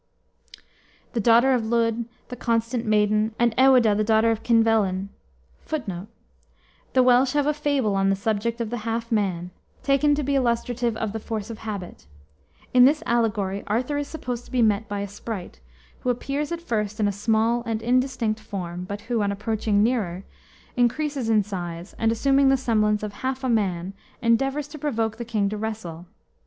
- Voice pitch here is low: No, high, 225 Hz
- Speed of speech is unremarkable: Yes, average, 185 wpm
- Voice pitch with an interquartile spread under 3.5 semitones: Yes, average, 3.1 semitones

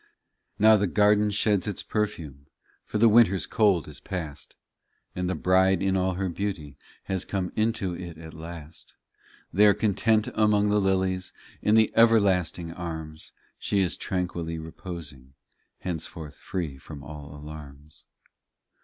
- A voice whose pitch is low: Yes, very low, 90 Hz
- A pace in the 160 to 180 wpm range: No, average, 145 wpm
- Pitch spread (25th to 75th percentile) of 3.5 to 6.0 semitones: Yes, average, 4.4 semitones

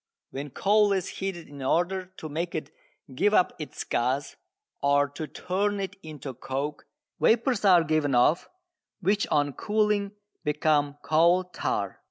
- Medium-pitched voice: Yes, medium, 165 Hz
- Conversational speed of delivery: Yes, average, 145 wpm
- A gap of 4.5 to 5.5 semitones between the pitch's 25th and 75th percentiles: Yes, average, 5.2 semitones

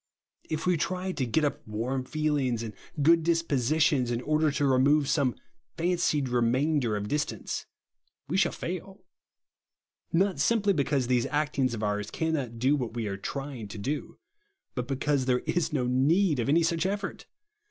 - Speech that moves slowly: No, average, 165 wpm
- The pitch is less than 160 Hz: Yes, medium, 140 Hz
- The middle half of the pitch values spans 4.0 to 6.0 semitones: Yes, average, 4.5 semitones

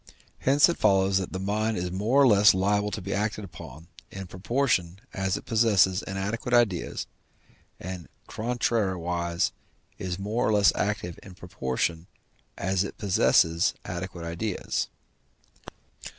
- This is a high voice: No, very low, 95 Hz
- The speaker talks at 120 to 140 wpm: Yes, slow, 135 wpm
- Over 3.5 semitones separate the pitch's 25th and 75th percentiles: No, average, 3.1 semitones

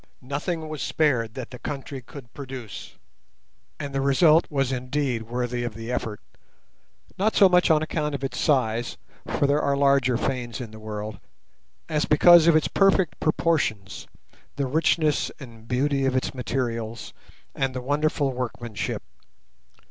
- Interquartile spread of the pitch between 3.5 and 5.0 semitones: Yes, average, 3.8 semitones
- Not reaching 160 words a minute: Yes, average, 145 wpm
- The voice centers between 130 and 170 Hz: Yes, low, 135 Hz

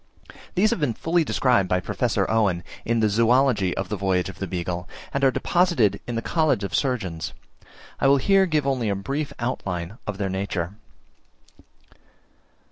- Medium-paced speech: Yes, average, 170 wpm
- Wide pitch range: Yes, wide, 6.3 semitones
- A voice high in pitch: No, low, 110 Hz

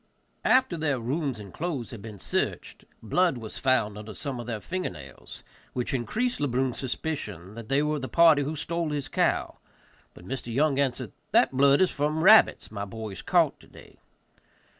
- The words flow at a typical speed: Yes, average, 180 wpm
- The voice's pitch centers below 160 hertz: Yes, low, 135 Hz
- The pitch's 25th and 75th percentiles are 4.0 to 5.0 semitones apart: No, wide, 5.5 semitones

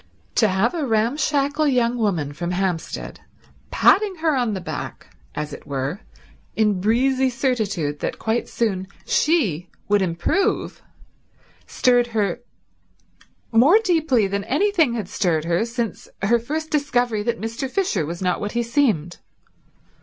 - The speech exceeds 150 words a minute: No, average, 140 wpm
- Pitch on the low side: No, high, 230 Hz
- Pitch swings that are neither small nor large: No, wide, 6.1 semitones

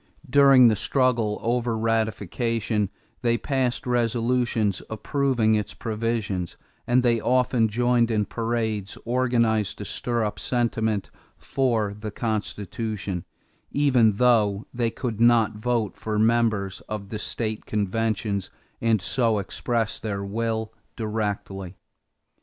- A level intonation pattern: Yes, narrow, 2.2 semitones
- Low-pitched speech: Yes, low, 115 Hz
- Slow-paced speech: Yes, slow, 115 wpm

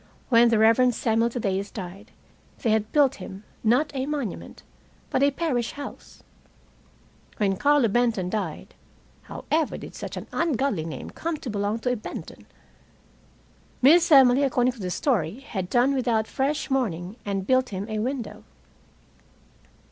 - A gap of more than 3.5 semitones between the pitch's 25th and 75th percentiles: Yes, average, 4.8 semitones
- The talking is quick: No, average, 150 wpm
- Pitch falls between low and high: No, high, 240 Hz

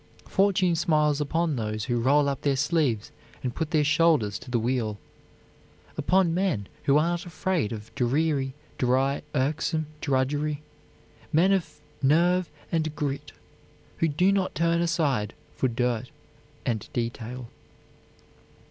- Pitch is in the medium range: Yes, medium, 145 Hz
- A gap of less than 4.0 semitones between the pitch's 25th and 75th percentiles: No, average, 4.8 semitones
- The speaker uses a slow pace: Yes, slow, 130 wpm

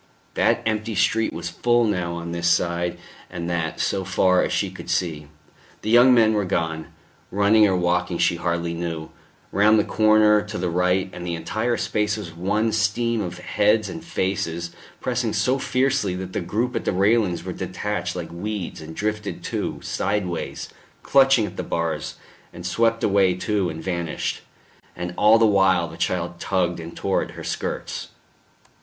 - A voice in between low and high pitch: No, very low, 95 Hz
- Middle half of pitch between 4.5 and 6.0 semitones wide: No, average, 3.8 semitones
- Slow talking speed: No, average, 175 wpm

